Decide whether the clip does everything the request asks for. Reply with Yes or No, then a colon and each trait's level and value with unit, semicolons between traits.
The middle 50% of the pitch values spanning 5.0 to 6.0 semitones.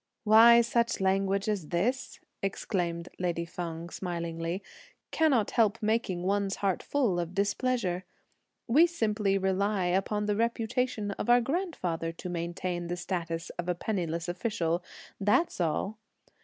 No: average, 4.1 semitones